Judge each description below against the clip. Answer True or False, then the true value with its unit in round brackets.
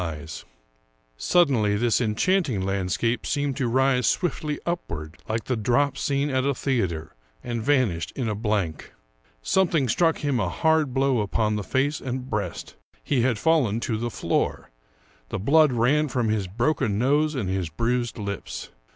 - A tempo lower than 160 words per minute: False (165 wpm)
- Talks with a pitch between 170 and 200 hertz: False (120 Hz)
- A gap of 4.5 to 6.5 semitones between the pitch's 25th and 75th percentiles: True (5.1 semitones)